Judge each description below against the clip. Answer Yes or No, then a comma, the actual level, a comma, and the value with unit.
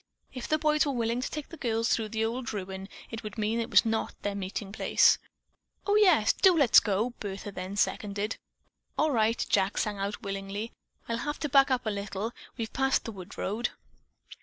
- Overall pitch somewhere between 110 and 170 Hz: No, high, 225 Hz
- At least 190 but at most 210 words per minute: Yes, average, 200 wpm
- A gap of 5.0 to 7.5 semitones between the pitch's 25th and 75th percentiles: No, average, 3.8 semitones